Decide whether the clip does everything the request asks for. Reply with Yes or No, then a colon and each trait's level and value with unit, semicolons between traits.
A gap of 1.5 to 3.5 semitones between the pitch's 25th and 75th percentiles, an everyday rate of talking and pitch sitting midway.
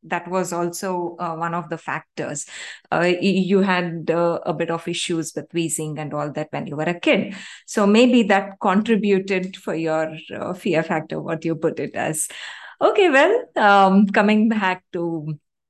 Yes: average, 3.2 semitones; average, 175 wpm; medium, 175 Hz